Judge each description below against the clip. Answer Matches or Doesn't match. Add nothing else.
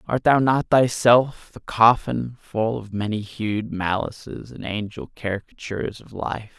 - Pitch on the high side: Doesn't match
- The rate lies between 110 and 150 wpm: Matches